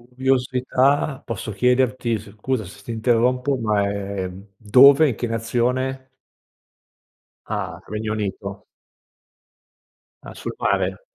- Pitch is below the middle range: Yes, low, 120 Hz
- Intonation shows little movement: No, average, 3.5 semitones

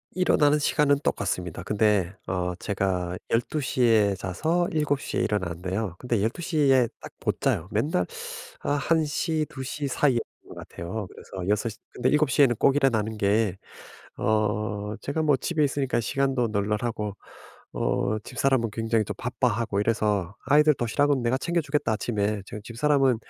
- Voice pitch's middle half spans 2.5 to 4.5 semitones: No, wide, 5.5 semitones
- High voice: No, low, 115 Hz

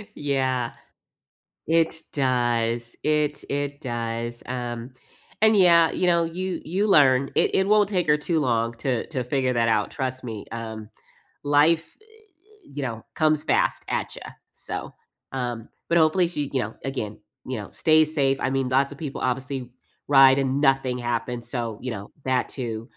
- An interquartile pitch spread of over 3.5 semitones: Yes, average, 4.6 semitones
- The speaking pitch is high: No, low, 135 Hz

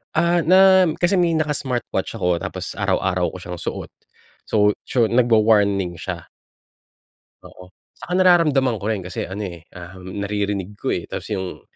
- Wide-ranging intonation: Yes, wide, 8.4 semitones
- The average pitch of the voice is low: Yes, low, 105 Hz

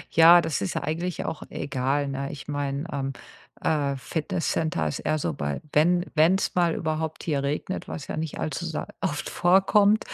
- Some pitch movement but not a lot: Yes, average, 3.4 semitones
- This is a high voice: No, medium, 155 Hz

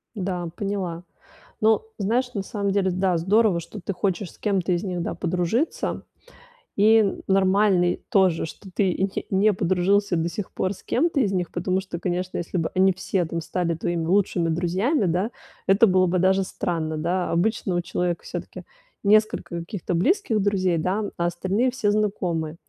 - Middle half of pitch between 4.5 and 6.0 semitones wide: No, average, 2.7 semitones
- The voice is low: No, medium, 185 Hz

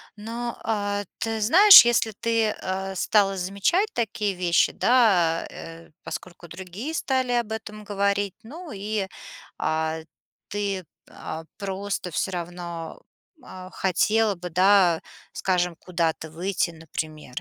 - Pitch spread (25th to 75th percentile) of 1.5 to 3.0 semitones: No, average, 4.0 semitones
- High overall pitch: Yes, high, 195 Hz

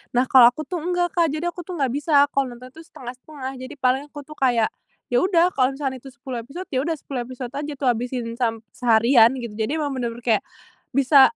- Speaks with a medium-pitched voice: No, very high, 265 Hz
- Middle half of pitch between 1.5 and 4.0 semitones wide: Yes, average, 3.5 semitones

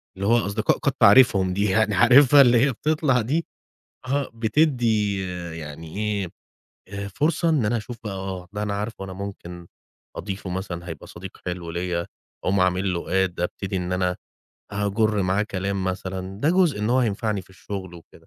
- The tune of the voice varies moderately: Yes, average, 3.7 semitones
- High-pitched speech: No, low, 100 Hz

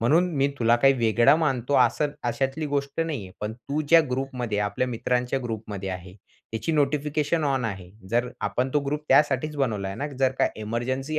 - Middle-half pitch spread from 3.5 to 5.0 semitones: Yes, average, 4.1 semitones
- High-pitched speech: No, low, 130 Hz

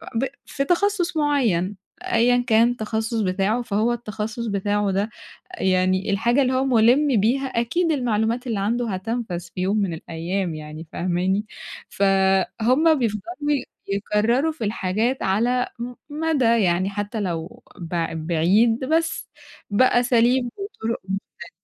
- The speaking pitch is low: No, high, 220 Hz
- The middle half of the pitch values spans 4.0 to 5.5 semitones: Yes, average, 4.6 semitones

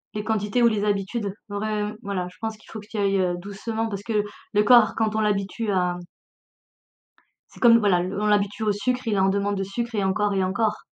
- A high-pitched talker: Yes, high, 205 Hz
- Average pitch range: No, narrow, 1.8 semitones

